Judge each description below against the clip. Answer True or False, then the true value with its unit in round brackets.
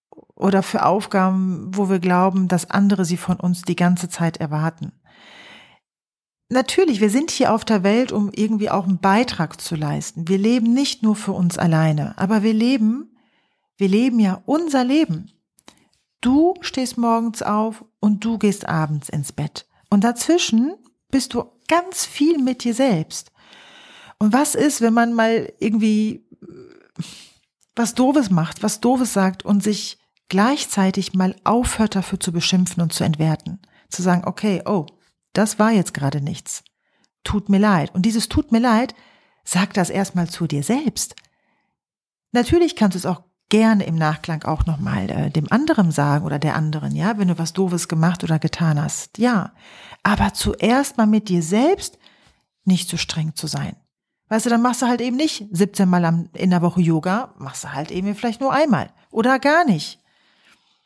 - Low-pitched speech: False (200 Hz)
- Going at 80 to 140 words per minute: False (170 wpm)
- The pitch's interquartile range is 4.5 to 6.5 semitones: True (4.8 semitones)